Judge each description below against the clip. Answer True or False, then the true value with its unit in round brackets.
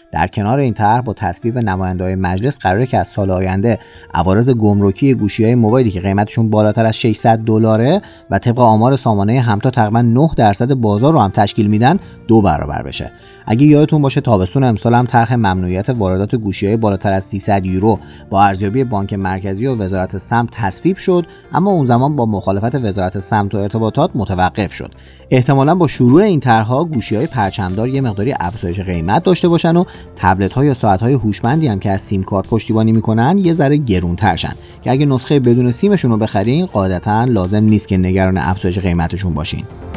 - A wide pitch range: False (4.8 semitones)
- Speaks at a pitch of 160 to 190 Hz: False (110 Hz)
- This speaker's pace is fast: True (185 wpm)